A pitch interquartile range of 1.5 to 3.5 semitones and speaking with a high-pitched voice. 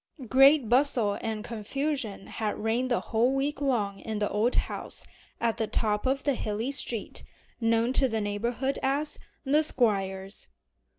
No: average, 4.1 semitones; high, 235 Hz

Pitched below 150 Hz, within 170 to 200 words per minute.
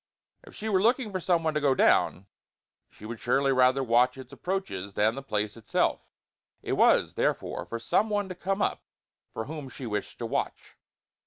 Yes: low, 135 Hz; average, 190 wpm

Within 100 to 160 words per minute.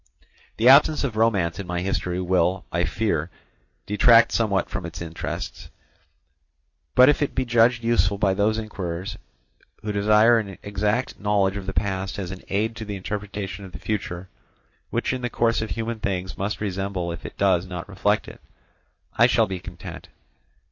No: average, 175 wpm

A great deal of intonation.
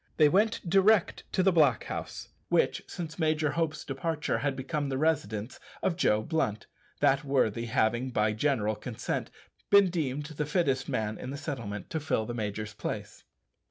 Yes: wide, 6.4 semitones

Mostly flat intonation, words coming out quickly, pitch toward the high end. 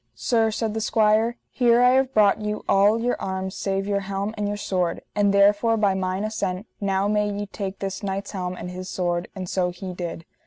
Yes: narrow, 2.1 semitones; fast, 210 wpm; high, 200 Hz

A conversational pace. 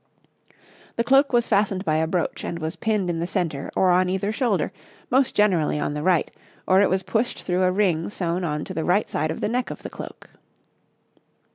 No: fast, 215 wpm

